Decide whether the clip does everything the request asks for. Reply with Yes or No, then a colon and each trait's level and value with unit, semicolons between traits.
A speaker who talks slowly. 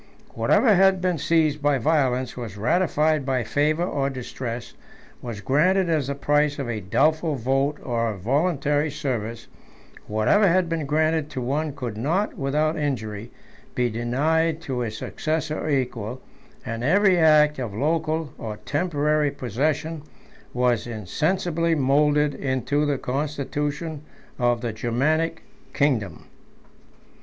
Yes: slow, 130 wpm